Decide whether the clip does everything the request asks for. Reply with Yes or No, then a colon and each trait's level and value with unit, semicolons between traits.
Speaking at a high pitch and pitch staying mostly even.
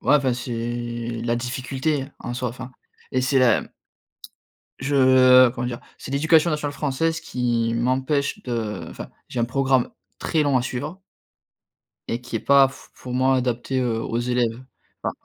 No: low, 130 Hz; narrow, 2.2 semitones